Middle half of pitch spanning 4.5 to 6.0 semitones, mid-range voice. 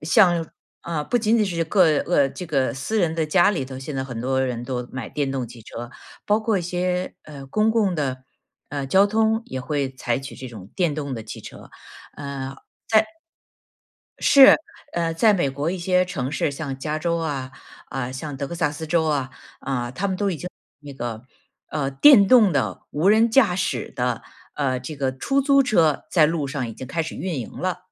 Yes: wide, 5.5 semitones; medium, 150 Hz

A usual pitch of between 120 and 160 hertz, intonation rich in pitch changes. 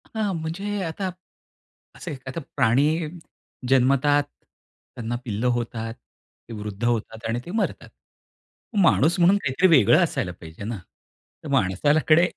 Yes: low, 135 Hz; wide, 7.0 semitones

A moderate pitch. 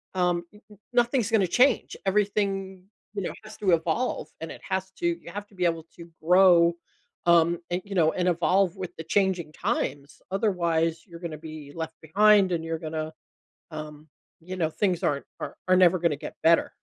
Yes: medium, 175 Hz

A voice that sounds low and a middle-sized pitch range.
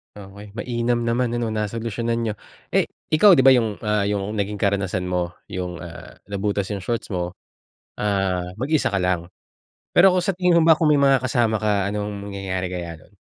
Yes: low, 105 Hz; average, 3.8 semitones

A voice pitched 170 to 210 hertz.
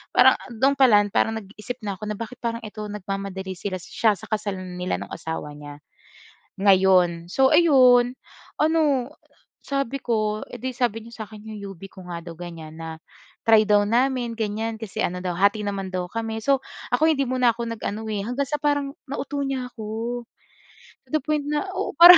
No: high, 220 Hz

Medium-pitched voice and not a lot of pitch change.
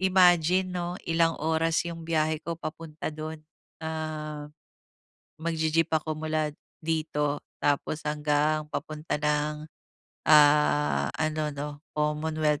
Yes: medium, 155 Hz; narrow, 1.3 semitones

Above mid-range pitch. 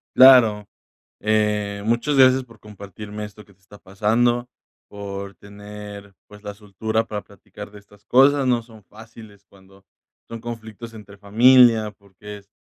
No: low, 105 Hz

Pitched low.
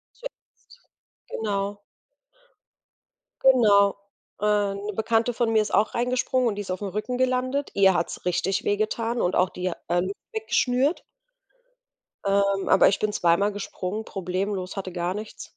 No: high, 205 Hz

